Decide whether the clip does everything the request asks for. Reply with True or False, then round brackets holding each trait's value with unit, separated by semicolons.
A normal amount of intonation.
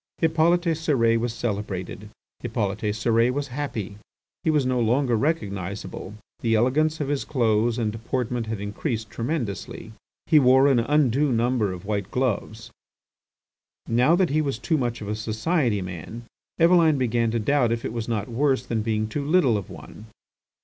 True (4.6 semitones)